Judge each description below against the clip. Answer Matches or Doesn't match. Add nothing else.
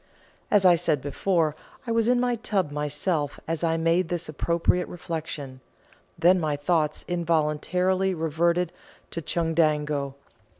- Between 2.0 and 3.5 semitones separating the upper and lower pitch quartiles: Matches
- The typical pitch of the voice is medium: Matches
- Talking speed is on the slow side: Matches